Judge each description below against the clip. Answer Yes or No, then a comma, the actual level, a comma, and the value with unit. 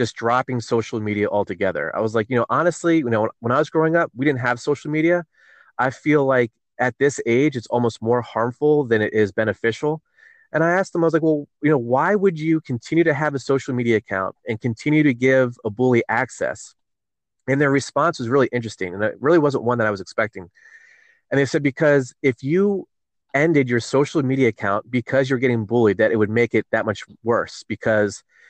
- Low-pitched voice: Yes, low, 130 Hz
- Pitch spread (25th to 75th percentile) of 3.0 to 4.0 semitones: No, average, 4.8 semitones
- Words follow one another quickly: Yes, fast, 220 wpm